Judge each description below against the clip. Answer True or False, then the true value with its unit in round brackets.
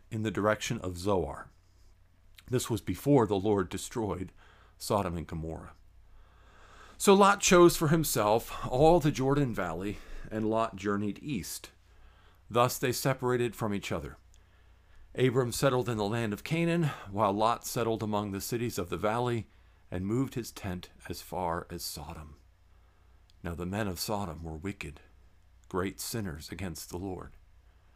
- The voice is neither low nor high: False (100 Hz)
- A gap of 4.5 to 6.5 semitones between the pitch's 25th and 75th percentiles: True (4.8 semitones)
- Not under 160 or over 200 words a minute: False (150 wpm)